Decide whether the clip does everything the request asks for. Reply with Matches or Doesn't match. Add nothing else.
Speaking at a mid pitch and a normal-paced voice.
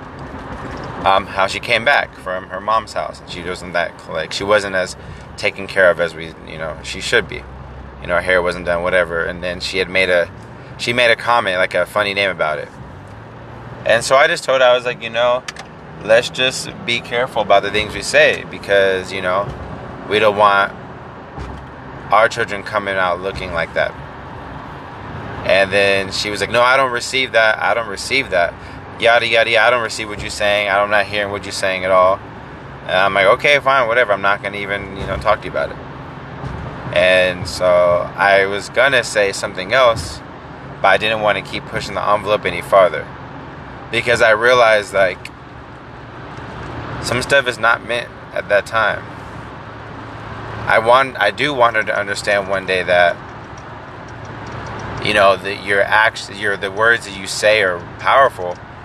Doesn't match